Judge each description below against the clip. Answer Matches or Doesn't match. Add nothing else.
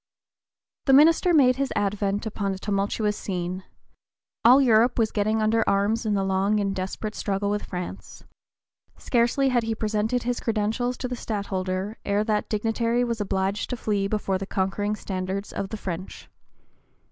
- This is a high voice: Matches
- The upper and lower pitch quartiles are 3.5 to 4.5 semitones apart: Doesn't match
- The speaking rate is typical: Matches